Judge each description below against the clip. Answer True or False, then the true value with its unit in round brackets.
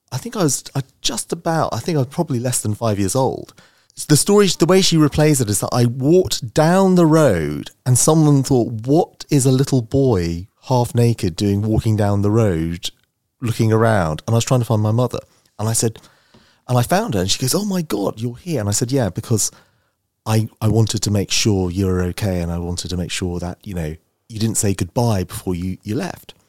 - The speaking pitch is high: False (115 Hz)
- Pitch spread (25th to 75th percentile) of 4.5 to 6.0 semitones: True (5.3 semitones)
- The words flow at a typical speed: False (230 wpm)